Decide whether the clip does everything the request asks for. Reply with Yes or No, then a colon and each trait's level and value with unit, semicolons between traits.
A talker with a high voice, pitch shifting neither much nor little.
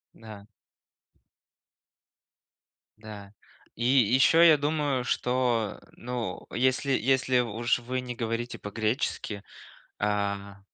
No: low, 120 Hz; average, 3.3 semitones